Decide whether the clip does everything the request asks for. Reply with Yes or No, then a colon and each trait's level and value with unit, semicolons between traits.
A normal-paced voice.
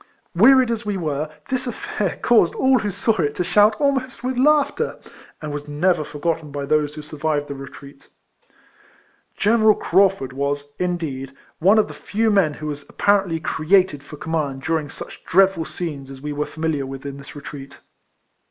Yes: average, 180 wpm